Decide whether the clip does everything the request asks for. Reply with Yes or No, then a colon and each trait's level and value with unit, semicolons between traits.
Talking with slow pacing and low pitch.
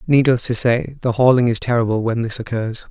No: fast, 205 wpm; low, 120 Hz